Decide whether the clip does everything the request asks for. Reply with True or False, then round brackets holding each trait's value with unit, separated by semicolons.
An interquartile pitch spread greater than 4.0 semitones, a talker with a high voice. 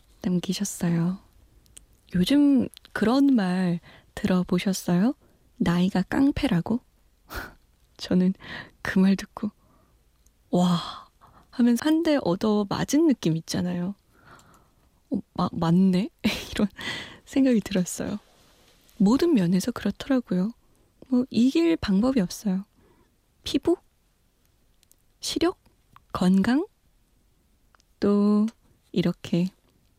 True (5.6 semitones; 195 Hz)